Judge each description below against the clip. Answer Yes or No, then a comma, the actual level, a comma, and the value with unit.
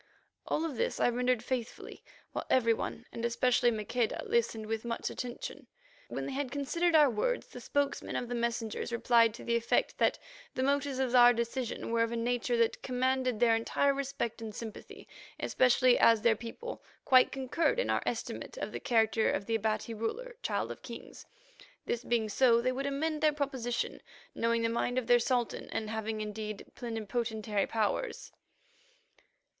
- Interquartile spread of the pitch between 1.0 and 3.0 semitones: Yes, narrow, 2.5 semitones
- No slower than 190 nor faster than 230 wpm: No, average, 175 wpm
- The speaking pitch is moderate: No, high, 240 Hz